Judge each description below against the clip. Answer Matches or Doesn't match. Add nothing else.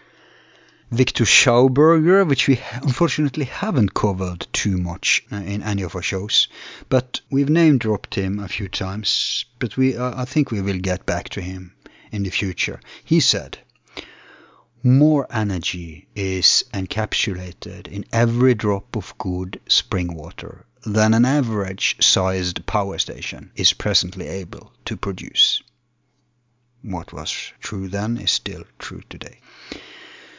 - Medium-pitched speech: Doesn't match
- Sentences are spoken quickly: Doesn't match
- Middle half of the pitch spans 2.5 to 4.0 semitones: Doesn't match